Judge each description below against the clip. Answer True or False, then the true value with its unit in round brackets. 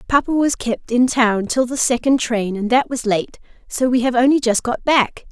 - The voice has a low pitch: False (245 Hz)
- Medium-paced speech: False (225 wpm)